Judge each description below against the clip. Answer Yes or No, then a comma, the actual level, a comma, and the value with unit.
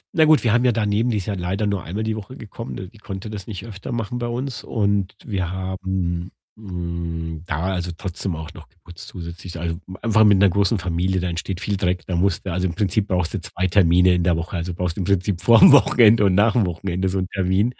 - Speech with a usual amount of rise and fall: Yes, average, 3.1 semitones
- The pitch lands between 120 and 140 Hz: No, very low, 95 Hz